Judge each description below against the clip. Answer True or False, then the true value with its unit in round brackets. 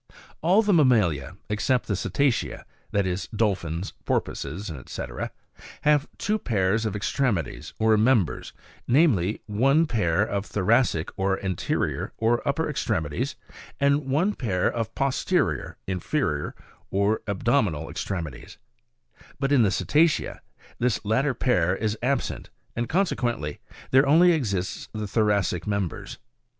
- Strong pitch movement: True (6.4 semitones)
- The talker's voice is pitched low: True (110 Hz)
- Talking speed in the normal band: False (130 wpm)